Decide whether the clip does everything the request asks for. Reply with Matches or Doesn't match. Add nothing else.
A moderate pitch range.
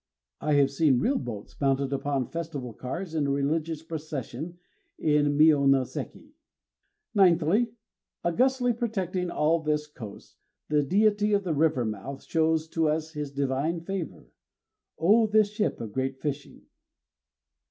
Matches